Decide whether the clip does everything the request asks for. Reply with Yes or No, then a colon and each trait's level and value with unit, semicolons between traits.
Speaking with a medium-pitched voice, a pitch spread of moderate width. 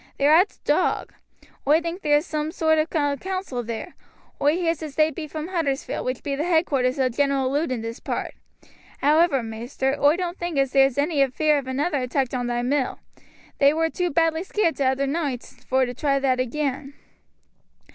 No: very high, 285 Hz; average, 3.4 semitones